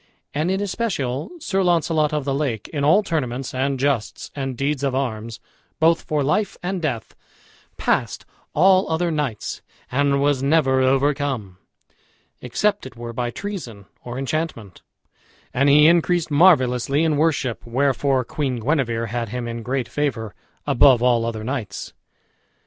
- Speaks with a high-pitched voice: No, medium, 140 Hz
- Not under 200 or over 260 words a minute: No, average, 145 wpm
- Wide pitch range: No, average, 4.2 semitones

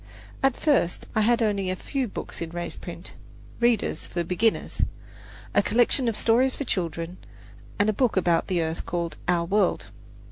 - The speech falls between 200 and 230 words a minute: No, average, 170 wpm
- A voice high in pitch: Yes, high, 200 Hz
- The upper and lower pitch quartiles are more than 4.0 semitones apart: Yes, wide, 5.4 semitones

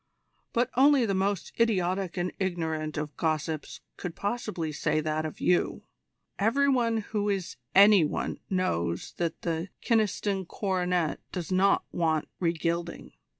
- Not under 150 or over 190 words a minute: No, average, 140 wpm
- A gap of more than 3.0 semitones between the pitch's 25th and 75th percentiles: Yes, average, 4.0 semitones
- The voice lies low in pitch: No, medium, 180 Hz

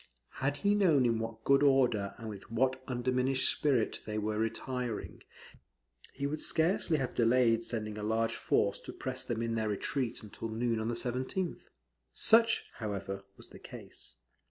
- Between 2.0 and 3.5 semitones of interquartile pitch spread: Yes, average, 3.2 semitones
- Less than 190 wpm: Yes, average, 165 wpm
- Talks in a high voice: No, low, 120 Hz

